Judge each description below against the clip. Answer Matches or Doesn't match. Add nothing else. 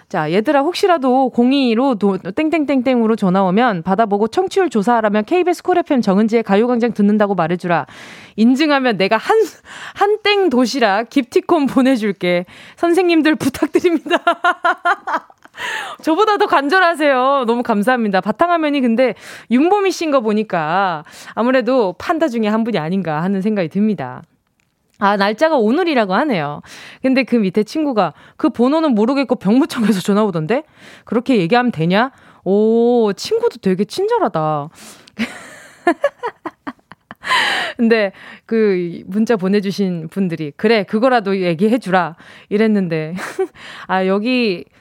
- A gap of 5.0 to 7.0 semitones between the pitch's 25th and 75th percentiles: Doesn't match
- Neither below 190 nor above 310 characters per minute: Matches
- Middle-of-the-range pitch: Doesn't match